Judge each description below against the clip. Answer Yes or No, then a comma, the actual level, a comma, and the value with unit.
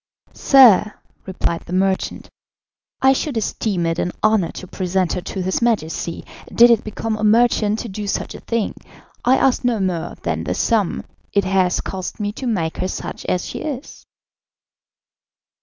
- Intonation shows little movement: No, average, 4.0 semitones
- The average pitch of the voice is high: Yes, high, 205 Hz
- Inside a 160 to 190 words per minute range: Yes, average, 170 wpm